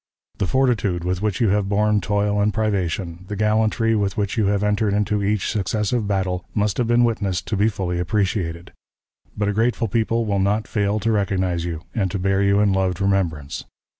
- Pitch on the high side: No, low, 100 Hz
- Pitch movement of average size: No, narrow, 2.1 semitones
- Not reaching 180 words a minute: No, average, 195 wpm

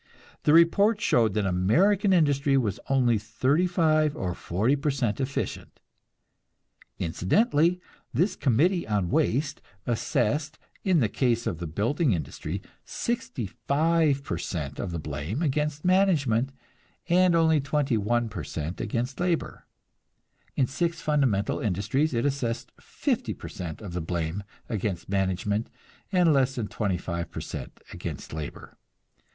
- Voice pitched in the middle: No, low, 130 Hz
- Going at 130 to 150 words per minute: Yes, average, 140 wpm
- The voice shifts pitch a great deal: Yes, wide, 7.5 semitones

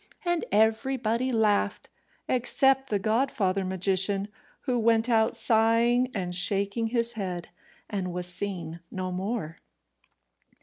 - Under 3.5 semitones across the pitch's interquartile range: No, average, 3.9 semitones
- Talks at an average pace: No, slow, 115 wpm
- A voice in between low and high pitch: No, high, 215 Hz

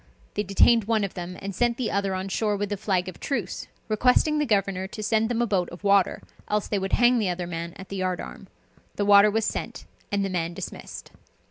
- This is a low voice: No, high, 200 Hz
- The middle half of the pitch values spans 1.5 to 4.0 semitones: Yes, average, 2.8 semitones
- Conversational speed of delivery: No, fast, 235 wpm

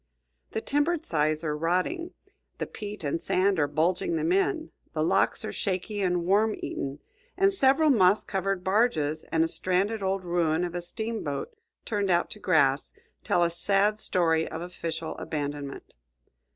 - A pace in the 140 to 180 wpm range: Yes, average, 160 wpm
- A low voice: No, medium, 185 Hz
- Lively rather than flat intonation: No, average, 5.0 semitones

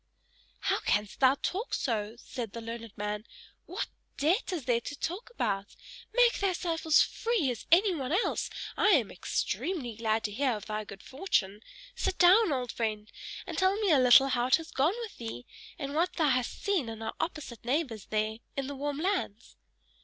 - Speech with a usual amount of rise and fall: No, wide, 7.6 semitones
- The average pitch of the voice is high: Yes, very high, 265 Hz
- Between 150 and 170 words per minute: No, average, 185 wpm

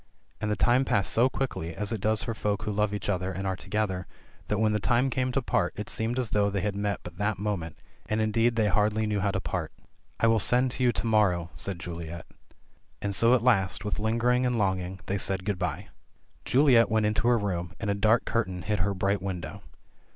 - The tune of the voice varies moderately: Yes, average, 3.1 semitones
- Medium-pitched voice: No, low, 105 Hz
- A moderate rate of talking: No, fast, 235 wpm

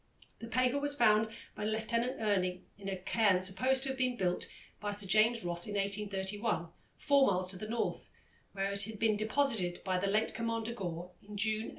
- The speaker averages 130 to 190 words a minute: No, average, 200 wpm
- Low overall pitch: No, high, 210 Hz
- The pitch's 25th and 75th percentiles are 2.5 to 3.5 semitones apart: Yes, average, 3.2 semitones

